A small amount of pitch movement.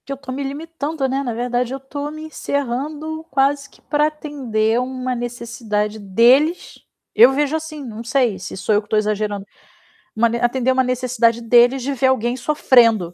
No: average, 3.4 semitones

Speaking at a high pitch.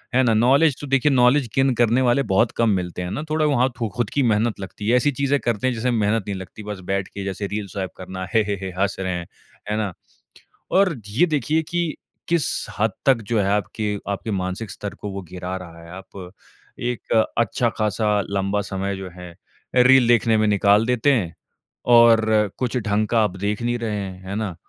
No: low, 110 Hz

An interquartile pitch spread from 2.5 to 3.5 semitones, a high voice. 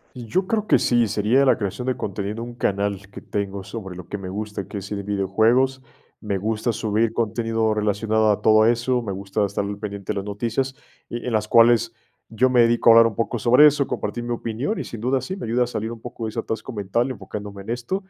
No: average, 2.8 semitones; low, 110 Hz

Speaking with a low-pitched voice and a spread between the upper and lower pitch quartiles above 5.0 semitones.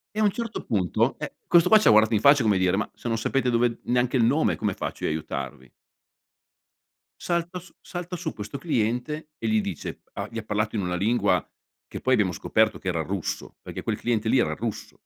Yes: low, 115 Hz; wide, 5.6 semitones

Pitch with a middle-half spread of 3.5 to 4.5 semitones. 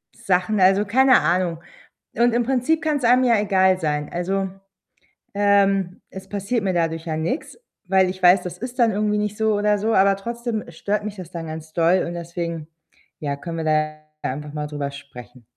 Yes: average, 4.2 semitones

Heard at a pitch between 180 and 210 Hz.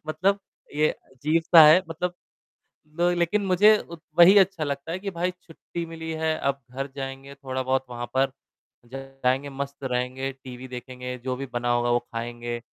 No: low, 135 Hz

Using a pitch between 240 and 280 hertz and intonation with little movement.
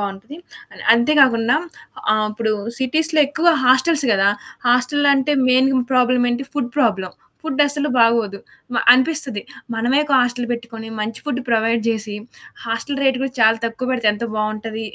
No: high, 245 Hz; average, 3.4 semitones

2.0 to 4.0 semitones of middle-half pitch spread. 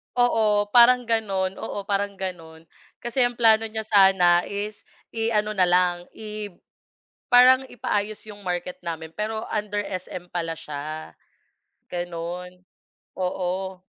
Yes: average, 3.5 semitones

